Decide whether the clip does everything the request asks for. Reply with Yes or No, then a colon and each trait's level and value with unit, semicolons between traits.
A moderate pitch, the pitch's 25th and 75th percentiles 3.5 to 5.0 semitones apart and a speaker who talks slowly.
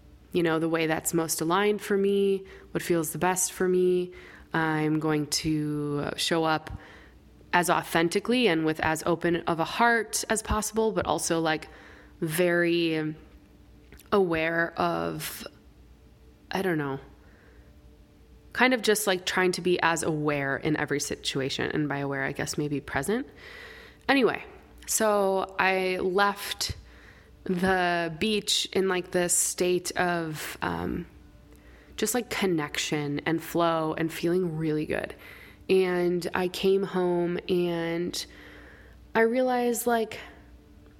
Yes: medium, 170 Hz; average, 4.0 semitones; slow, 130 wpm